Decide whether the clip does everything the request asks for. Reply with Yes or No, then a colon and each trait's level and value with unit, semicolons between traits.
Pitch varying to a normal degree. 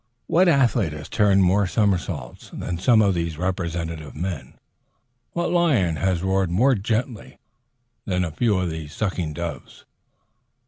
Yes: average, 4.3 semitones